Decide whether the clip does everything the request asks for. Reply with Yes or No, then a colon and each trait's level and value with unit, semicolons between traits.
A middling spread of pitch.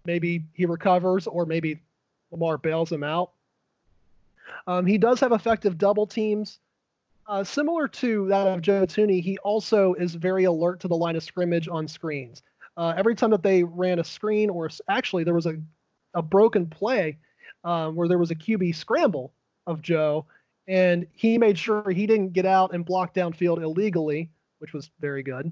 Yes: average, 3.6 semitones